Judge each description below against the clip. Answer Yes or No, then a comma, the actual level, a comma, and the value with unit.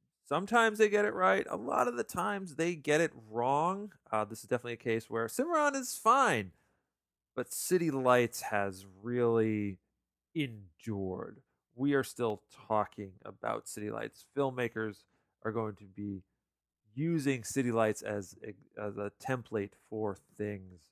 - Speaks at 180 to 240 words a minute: No, average, 150 wpm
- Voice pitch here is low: Yes, low, 115 Hz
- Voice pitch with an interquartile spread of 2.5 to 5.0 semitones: No, wide, 5.6 semitones